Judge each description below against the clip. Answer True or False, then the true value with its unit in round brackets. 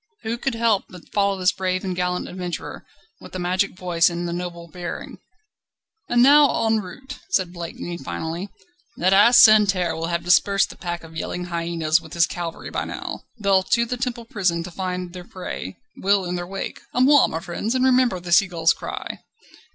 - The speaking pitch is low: False (180 Hz)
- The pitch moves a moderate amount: True (3.2 semitones)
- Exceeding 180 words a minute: True (190 wpm)